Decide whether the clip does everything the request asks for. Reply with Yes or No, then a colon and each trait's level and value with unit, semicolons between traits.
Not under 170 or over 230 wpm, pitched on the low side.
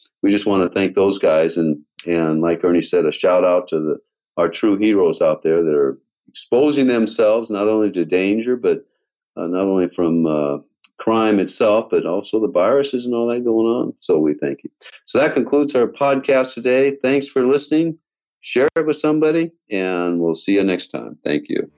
Yes: average, 200 wpm; low, 115 Hz